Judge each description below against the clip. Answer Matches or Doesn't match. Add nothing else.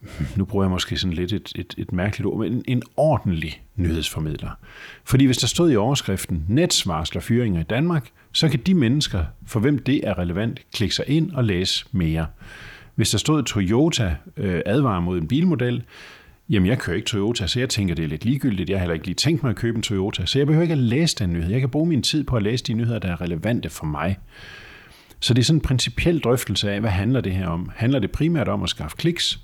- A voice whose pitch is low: Matches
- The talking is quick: Matches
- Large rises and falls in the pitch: Matches